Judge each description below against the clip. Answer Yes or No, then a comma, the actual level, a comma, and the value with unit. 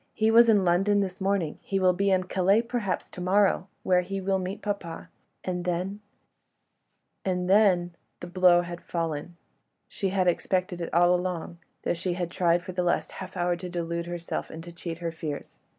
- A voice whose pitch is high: No, medium, 180 Hz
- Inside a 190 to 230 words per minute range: Yes, average, 195 wpm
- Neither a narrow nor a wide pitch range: No, narrow, 1.8 semitones